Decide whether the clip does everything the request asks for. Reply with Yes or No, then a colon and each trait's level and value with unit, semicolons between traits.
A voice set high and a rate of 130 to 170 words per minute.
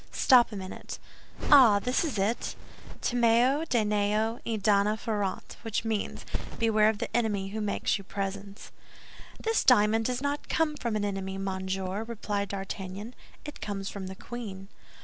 Yes: high, 210 Hz; average, 150 wpm